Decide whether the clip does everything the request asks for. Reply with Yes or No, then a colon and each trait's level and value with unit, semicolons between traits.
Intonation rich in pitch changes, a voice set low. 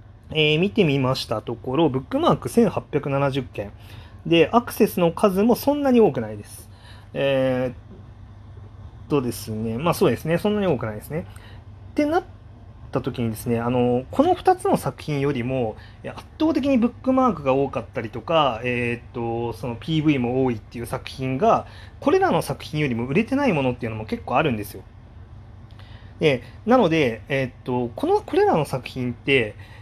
Yes: wide, 6.8 semitones; low, 130 Hz